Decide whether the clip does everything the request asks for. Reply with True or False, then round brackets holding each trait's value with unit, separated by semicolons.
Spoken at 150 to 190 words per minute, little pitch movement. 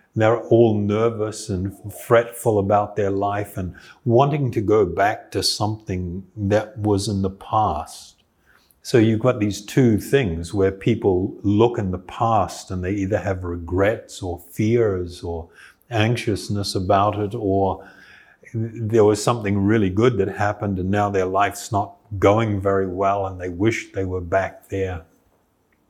True (155 wpm; 2.2 semitones)